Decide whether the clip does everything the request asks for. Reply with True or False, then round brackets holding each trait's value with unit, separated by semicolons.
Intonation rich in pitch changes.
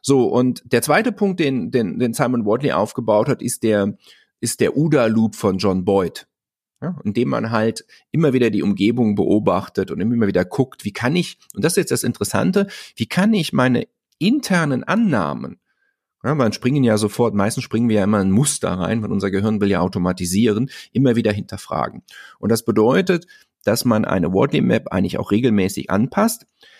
True (6.1 semitones)